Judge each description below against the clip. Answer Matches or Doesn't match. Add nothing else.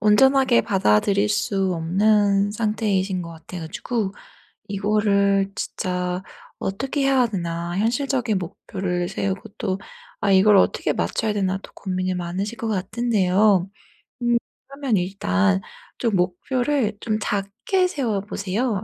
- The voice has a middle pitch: Doesn't match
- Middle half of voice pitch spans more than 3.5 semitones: Doesn't match